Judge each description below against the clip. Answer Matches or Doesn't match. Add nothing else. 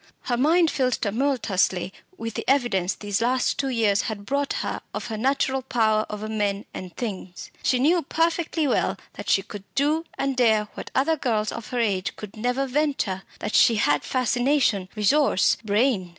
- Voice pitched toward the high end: Matches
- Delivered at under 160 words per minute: Doesn't match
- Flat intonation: Doesn't match